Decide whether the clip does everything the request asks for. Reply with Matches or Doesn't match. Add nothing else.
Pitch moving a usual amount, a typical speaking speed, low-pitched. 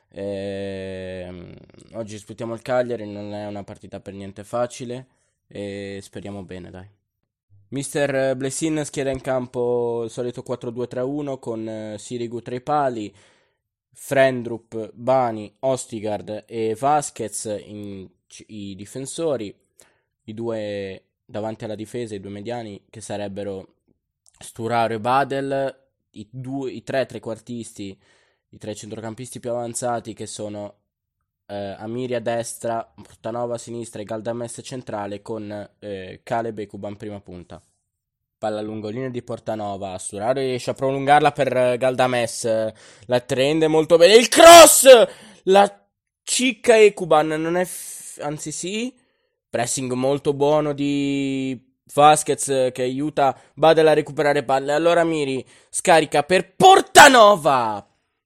Matches